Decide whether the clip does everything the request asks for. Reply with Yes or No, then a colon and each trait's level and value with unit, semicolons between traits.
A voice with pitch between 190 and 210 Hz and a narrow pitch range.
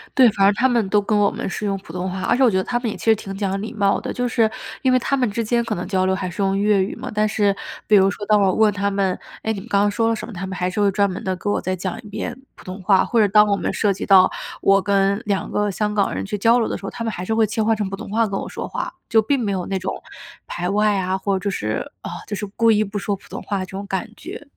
Yes: high, 205 Hz; narrow, 2.2 semitones